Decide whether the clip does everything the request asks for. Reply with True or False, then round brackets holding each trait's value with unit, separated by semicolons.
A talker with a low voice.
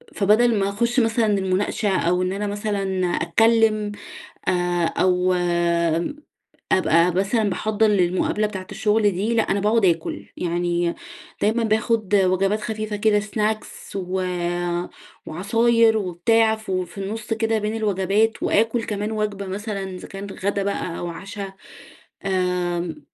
False (200 Hz)